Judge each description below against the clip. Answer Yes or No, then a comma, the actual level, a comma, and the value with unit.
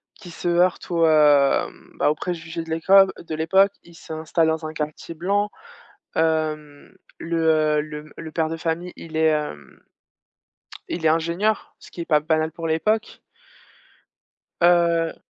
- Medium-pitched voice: Yes, medium, 160 Hz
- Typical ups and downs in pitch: No, narrow, 1.6 semitones